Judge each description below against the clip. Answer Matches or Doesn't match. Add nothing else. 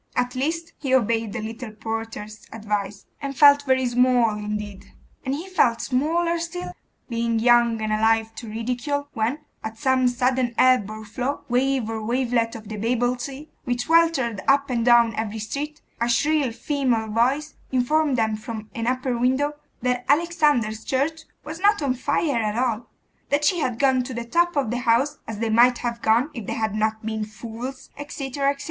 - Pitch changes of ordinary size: Matches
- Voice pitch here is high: Matches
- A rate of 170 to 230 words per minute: Matches